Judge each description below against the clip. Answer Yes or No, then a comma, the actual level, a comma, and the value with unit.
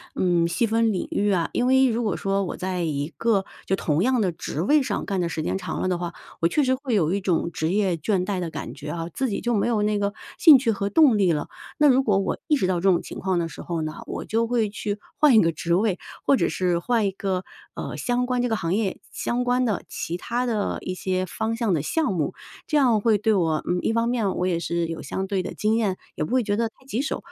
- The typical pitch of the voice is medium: No, high, 200 Hz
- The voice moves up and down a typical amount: Yes, average, 4.8 semitones